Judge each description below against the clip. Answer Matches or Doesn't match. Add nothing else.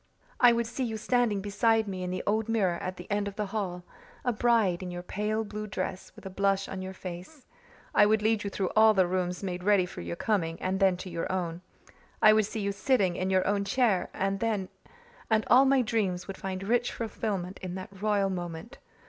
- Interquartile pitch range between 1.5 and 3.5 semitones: Matches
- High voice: Matches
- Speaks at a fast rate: Matches